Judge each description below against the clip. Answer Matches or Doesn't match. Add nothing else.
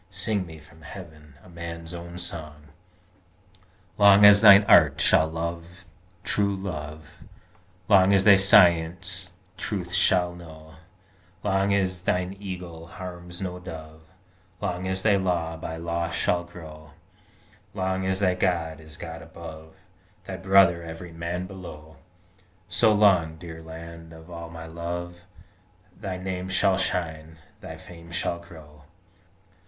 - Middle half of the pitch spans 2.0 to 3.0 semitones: Matches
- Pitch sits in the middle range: Doesn't match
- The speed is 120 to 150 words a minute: Matches